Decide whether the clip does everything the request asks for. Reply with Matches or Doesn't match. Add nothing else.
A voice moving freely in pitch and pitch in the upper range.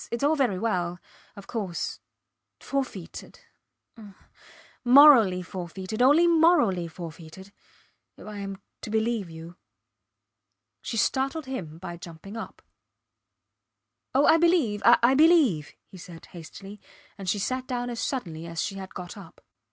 Matches